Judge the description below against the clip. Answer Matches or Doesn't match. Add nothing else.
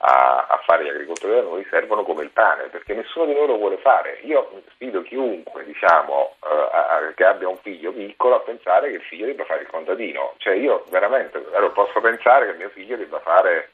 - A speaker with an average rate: Doesn't match